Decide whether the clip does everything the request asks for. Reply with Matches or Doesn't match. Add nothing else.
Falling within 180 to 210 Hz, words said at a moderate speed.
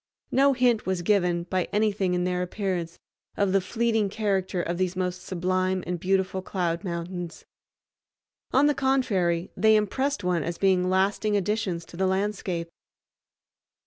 Matches